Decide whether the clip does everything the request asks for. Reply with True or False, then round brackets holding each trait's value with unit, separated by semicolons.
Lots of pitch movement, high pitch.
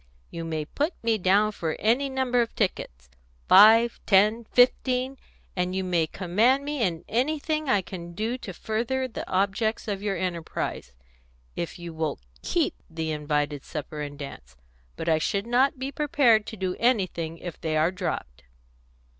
True (6.4 semitones; 195 Hz)